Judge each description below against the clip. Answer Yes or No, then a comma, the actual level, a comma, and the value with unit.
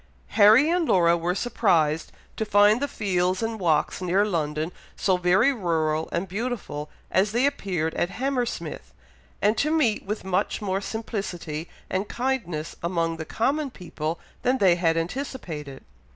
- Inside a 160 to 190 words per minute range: No, average, 150 wpm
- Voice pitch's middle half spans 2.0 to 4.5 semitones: No, average, 5.3 semitones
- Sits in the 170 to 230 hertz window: Yes, high, 190 Hz